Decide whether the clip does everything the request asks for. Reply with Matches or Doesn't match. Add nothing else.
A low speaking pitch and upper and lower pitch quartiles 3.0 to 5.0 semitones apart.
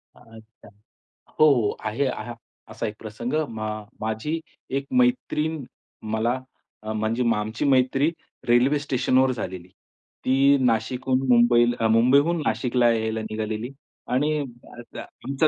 Matches